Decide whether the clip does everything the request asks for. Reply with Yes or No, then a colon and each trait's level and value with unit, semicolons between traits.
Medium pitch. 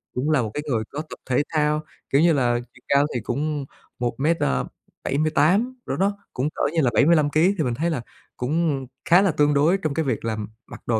Yes: medium, 150 Hz